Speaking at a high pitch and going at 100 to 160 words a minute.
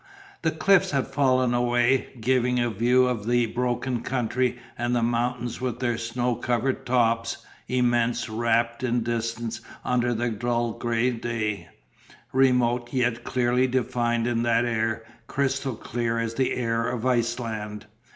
No: low, 120 Hz; average, 140 wpm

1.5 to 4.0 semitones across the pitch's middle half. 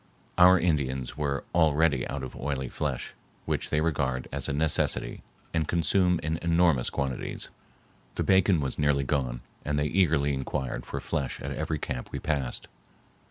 Yes: average, 3.6 semitones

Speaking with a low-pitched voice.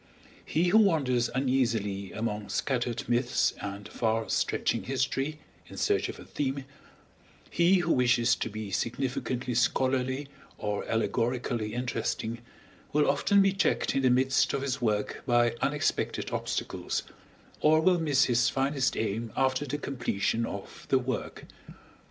Yes: low, 125 Hz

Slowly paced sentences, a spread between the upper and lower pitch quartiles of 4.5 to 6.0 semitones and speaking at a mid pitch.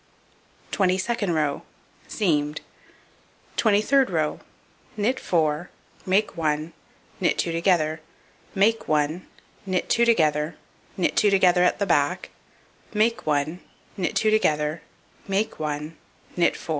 Yes: slow, 120 wpm; average, 4.9 semitones; medium, 175 Hz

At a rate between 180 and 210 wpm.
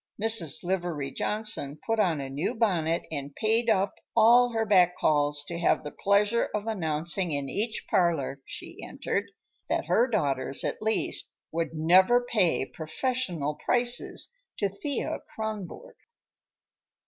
No: slow, 135 wpm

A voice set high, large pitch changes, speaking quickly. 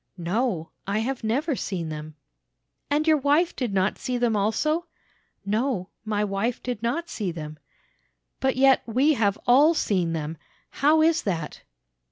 No: high, 225 Hz; wide, 6.4 semitones; average, 155 wpm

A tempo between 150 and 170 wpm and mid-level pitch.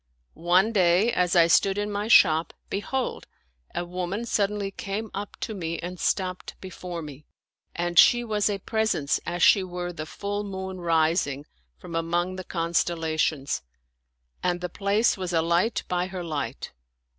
Yes: average, 165 wpm; medium, 180 Hz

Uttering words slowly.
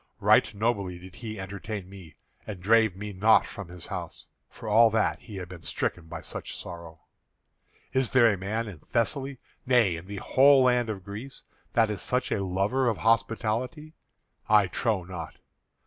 No: average, 175 wpm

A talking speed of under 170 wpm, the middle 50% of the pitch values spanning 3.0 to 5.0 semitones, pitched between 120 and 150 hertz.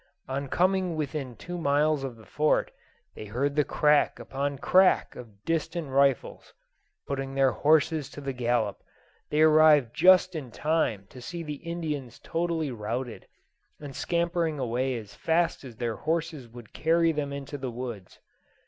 Yes: average, 155 wpm; average, 4.3 semitones; medium, 140 Hz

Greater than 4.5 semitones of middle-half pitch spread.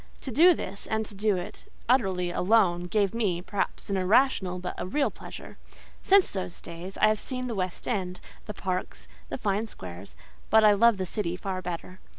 No: average, 3.4 semitones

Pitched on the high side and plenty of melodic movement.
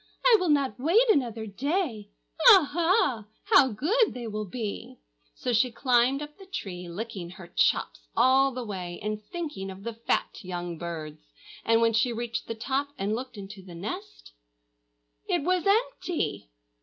Yes: high, 235 Hz; wide, 6.3 semitones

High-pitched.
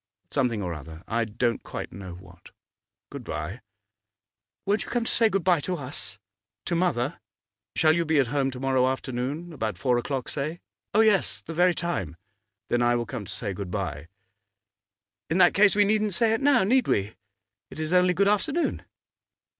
No: medium, 140 Hz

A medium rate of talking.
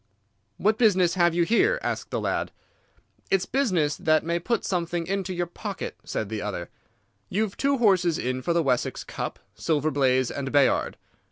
Yes: average, 165 wpm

